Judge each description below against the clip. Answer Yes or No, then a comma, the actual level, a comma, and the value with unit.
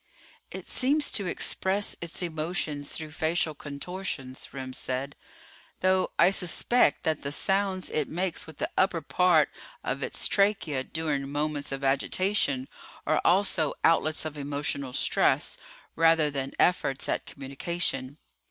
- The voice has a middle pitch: Yes, medium, 155 Hz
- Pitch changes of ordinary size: Yes, average, 4.5 semitones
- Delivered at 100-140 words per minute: Yes, slow, 135 wpm